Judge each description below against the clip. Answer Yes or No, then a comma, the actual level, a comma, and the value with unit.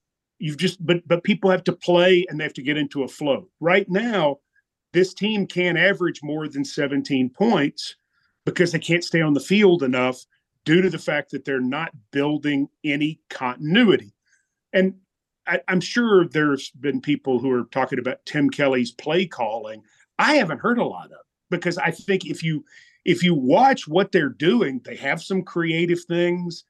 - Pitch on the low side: No, medium, 170 Hz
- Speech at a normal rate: Yes, average, 180 wpm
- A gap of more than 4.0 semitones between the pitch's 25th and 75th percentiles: Yes, average, 4.4 semitones